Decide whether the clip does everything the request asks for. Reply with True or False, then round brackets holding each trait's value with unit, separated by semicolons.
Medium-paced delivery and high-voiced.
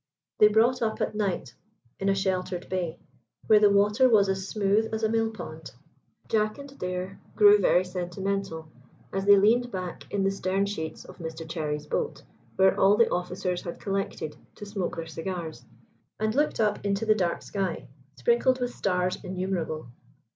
True (170 wpm; 195 Hz)